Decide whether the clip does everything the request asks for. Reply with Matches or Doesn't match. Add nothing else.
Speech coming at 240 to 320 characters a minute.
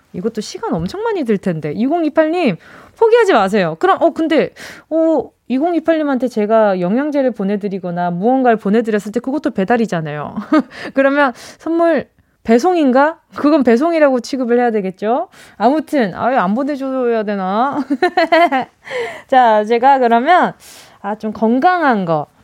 Matches